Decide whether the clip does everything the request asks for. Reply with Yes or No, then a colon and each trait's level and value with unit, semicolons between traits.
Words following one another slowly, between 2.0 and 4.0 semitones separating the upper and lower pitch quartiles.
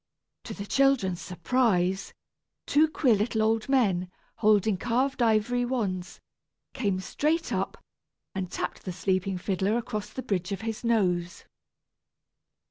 No: slow, 130 wpm; average, 4.6 semitones